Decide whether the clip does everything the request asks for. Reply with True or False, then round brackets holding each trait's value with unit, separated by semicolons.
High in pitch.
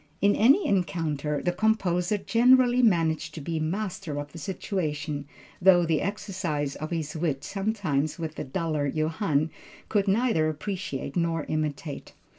False (165 Hz)